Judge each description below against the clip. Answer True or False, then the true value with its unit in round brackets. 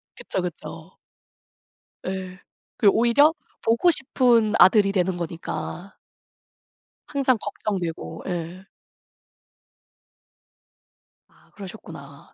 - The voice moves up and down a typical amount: True (4.7 semitones)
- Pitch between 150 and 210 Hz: True (190 Hz)